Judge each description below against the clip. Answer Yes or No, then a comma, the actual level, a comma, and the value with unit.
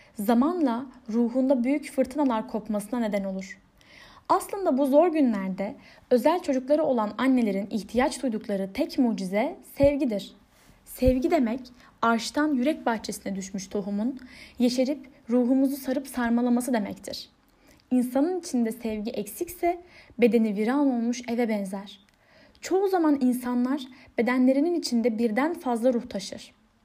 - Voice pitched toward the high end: Yes, very high, 250 Hz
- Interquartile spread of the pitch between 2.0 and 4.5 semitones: Yes, average, 4.1 semitones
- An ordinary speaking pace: Yes, average, 110 wpm